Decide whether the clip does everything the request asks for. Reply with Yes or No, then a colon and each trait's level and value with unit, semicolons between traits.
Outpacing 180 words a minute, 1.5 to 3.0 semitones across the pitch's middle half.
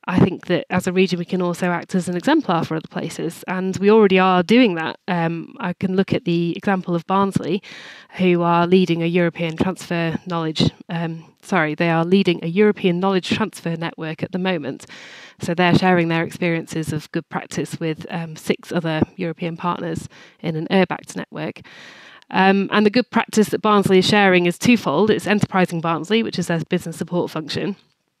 Yes: average, 190 wpm; narrow, 2.5 semitones